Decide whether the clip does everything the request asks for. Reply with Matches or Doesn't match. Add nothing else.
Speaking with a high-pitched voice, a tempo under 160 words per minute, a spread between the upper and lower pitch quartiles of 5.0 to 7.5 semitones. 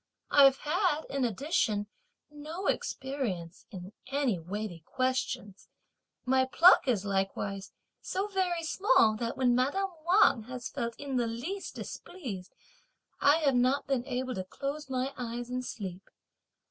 Matches